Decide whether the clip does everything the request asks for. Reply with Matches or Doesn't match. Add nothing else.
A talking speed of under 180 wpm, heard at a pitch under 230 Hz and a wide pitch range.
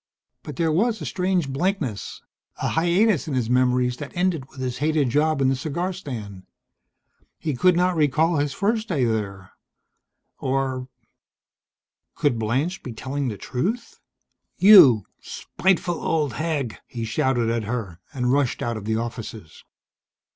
Matches